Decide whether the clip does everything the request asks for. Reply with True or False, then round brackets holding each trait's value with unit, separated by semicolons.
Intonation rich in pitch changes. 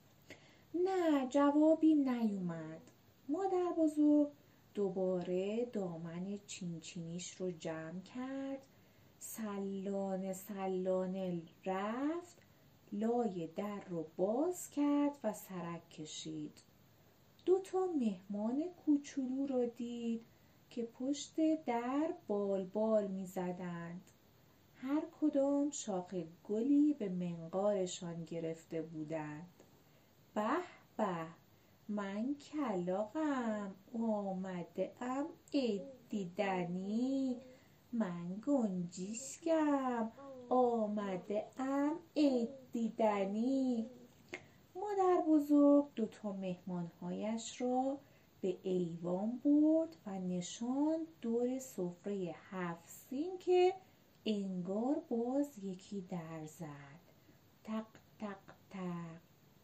True (7.0 semitones)